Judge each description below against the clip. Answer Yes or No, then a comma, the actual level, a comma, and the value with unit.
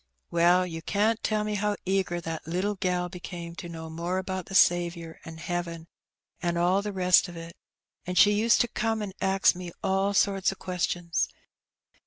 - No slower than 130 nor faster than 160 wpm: No, average, 180 wpm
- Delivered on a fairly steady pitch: Yes, narrow, 2.2 semitones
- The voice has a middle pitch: Yes, medium, 180 Hz